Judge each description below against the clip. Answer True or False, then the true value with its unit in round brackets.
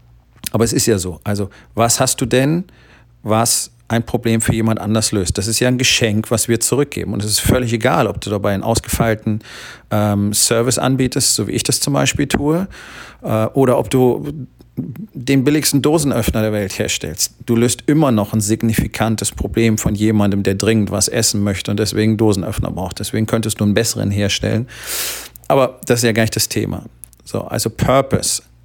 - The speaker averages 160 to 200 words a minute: True (190 wpm)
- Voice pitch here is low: True (115 Hz)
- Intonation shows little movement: False (3.0 semitones)